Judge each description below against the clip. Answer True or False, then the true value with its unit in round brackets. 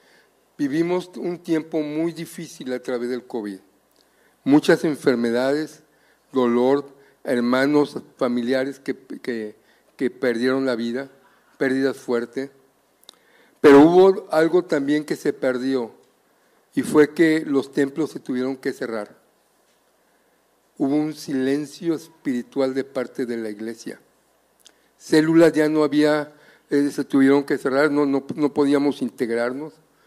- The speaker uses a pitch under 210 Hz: True (140 Hz)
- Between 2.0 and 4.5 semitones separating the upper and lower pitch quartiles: True (3.0 semitones)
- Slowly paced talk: True (120 wpm)